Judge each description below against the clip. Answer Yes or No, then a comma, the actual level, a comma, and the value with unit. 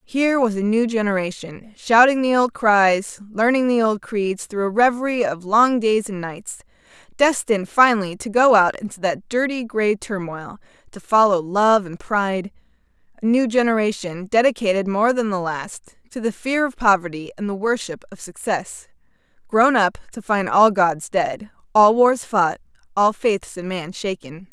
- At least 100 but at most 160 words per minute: No, average, 170 wpm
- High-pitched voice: Yes, high, 210 Hz